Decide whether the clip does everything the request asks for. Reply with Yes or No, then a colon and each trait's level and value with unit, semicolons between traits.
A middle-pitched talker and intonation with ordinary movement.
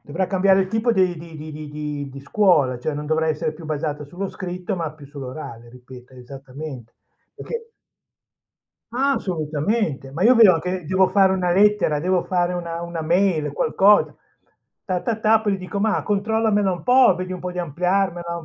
Yes: medium, 175 Hz; average, 4.5 semitones